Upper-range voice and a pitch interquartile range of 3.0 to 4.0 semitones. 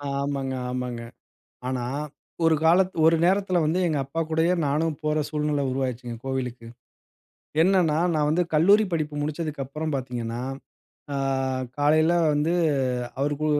No: medium, 150 Hz; average, 3.5 semitones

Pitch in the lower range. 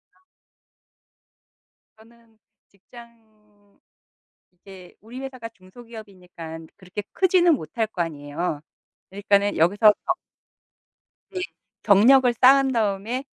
No: high, 215 Hz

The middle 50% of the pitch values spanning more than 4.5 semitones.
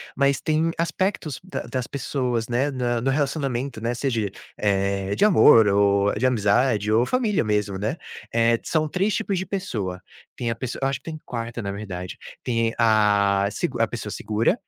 Yes: average, 5.2 semitones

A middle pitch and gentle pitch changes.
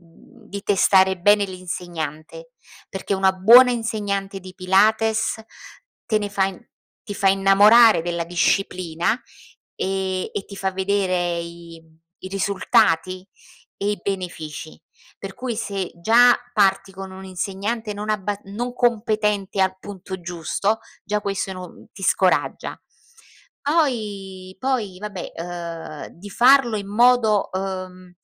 No: high, 195 Hz; narrow, 2.3 semitones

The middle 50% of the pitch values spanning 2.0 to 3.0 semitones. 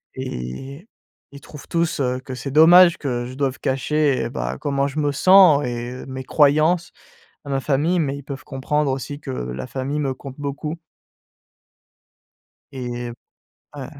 Yes: narrow, 2.6 semitones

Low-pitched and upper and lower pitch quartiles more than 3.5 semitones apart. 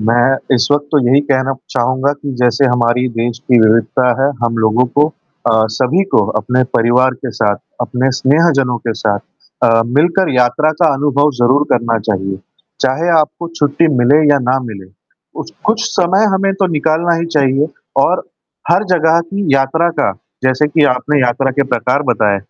Yes: low, 130 Hz; average, 3.9 semitones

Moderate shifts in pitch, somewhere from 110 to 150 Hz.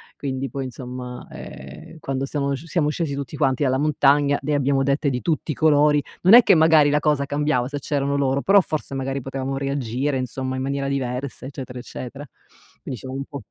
No: narrow, 1.9 semitones; medium, 140 Hz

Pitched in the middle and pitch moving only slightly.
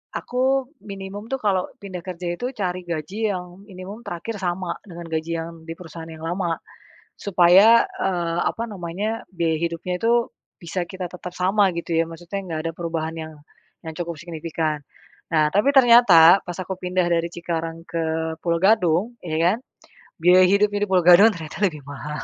No: medium, 180 Hz; average, 3.1 semitones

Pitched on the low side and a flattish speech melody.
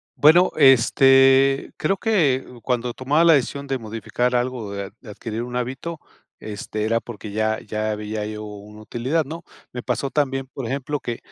No: low, 125 Hz; average, 4.0 semitones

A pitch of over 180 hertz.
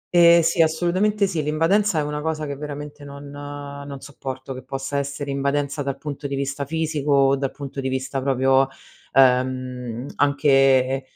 No: medium, 140 Hz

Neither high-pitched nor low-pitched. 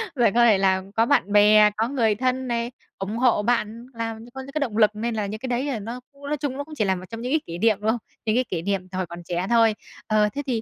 No: high, 225 Hz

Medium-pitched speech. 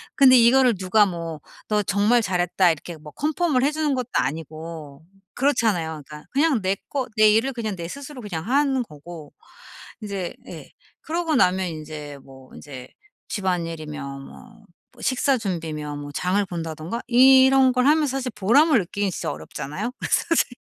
No: high, 200 Hz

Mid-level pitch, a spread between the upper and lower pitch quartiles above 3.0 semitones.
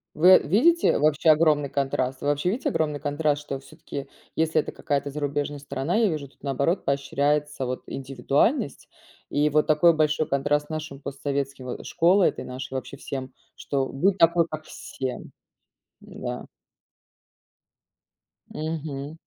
No: medium, 145 Hz; narrow, 2.4 semitones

